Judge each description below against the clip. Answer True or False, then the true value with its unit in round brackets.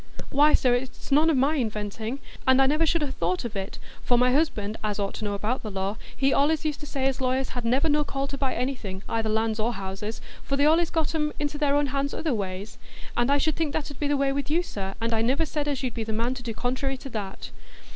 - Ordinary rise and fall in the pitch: True (4.7 semitones)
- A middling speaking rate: False (255 wpm)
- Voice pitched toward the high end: True (260 Hz)